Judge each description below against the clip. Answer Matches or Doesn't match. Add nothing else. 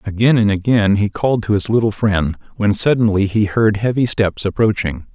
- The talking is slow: Doesn't match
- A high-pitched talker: Doesn't match